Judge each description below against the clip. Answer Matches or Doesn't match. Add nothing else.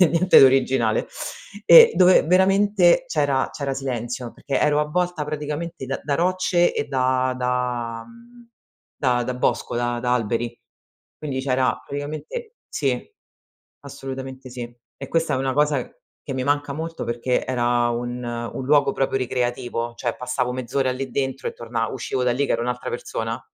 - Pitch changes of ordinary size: Matches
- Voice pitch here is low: Matches